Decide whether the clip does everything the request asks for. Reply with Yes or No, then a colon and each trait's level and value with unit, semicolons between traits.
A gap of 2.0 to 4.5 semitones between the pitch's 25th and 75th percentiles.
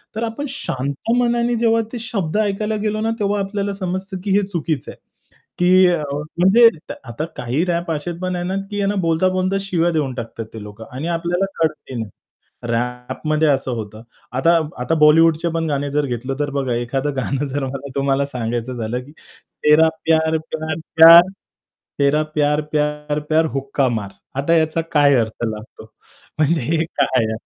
No: average, 5.2 semitones